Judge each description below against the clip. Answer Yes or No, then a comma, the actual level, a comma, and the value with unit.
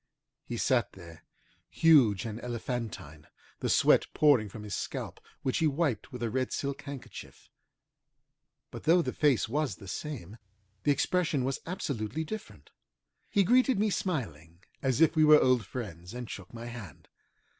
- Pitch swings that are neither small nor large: No, wide, 6.0 semitones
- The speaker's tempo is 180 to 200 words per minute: No, average, 155 wpm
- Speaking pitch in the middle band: No, low, 125 Hz